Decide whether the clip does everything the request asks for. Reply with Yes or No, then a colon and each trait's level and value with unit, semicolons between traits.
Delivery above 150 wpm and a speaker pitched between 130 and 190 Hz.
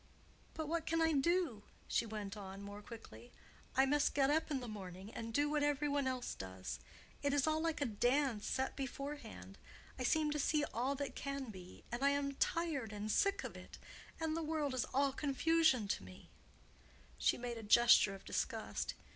No: average, 190 wpm; very high, 270 Hz